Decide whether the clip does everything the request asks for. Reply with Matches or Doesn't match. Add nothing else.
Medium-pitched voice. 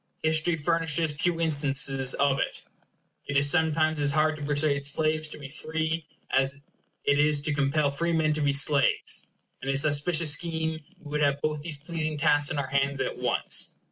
Matches